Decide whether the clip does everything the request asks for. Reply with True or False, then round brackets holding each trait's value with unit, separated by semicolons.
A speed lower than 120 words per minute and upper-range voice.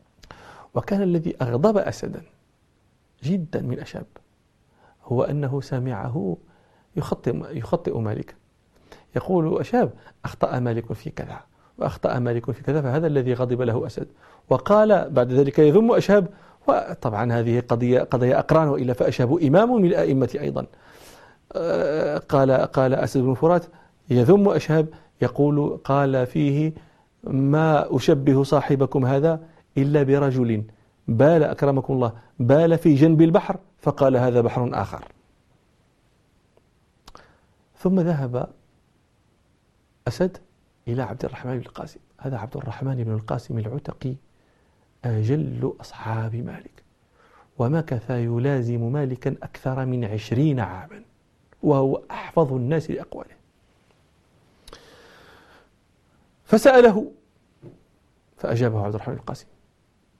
False (105 wpm; 135 Hz)